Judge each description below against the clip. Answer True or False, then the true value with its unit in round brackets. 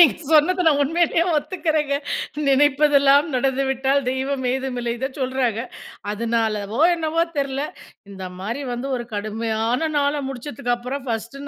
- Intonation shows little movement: False (3.6 semitones)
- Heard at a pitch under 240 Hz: False (265 Hz)